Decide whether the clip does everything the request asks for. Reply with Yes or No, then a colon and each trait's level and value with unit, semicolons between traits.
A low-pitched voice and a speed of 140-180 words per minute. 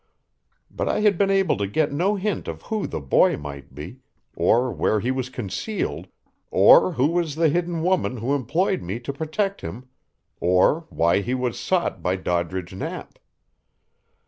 Yes: low, 130 Hz; average, 170 wpm